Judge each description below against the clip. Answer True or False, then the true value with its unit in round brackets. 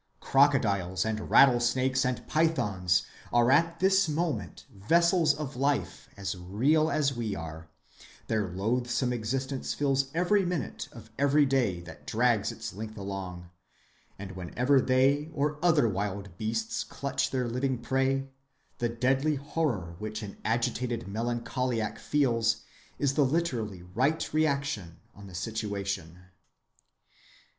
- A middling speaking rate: False (125 wpm)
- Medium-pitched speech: False (125 Hz)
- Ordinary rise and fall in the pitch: False (5.8 semitones)